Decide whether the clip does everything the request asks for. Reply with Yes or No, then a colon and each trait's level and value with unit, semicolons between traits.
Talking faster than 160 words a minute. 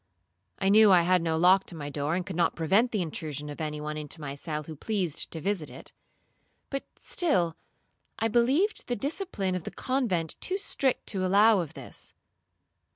Yes: average, 190 wpm